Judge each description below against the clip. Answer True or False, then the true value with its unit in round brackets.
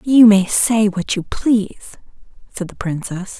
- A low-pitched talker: False (205 Hz)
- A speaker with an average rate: True (160 wpm)